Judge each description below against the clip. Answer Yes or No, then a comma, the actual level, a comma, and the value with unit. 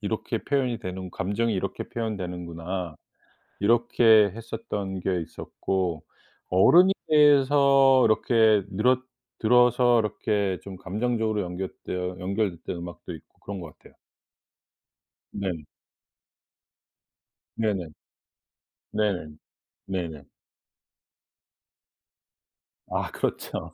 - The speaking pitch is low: Yes, low, 100 Hz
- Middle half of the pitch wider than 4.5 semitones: No, average, 4.1 semitones